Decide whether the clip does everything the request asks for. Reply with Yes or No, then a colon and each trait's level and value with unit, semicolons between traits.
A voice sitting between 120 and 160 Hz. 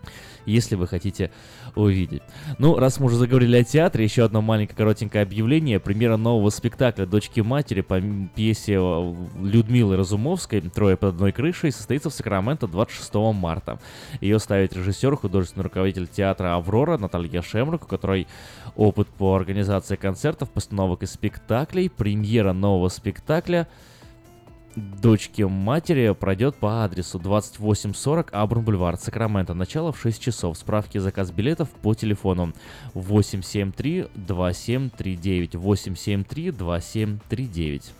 No: low, 105 Hz